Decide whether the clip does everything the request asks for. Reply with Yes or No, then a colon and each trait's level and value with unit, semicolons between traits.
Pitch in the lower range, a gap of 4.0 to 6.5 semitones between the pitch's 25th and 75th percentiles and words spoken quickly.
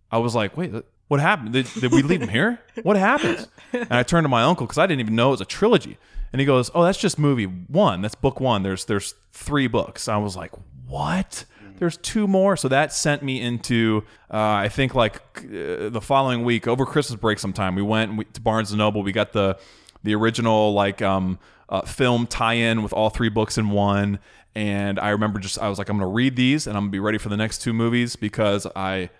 Yes: low, 110 Hz; average, 4.4 semitones; fast, 230 wpm